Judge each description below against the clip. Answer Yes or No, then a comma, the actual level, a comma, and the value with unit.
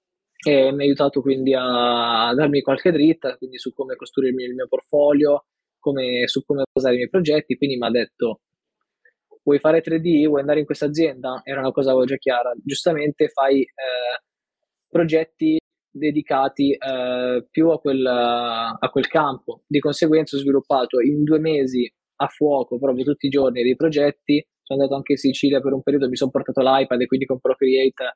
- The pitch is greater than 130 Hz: Yes, medium, 140 Hz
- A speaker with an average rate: No, fast, 175 wpm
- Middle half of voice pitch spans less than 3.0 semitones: Yes, narrow, 2.5 semitones